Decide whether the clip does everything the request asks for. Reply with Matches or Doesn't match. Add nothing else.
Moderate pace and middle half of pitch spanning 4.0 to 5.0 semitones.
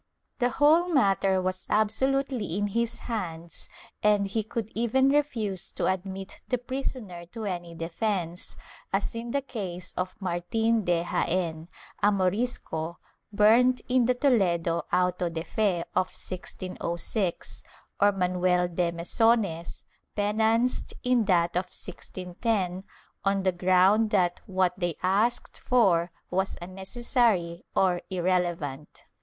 Doesn't match